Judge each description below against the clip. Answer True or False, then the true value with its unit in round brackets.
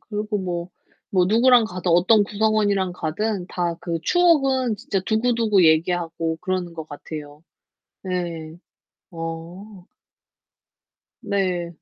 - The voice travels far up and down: False (4.1 semitones)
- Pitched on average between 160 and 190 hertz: True (185 Hz)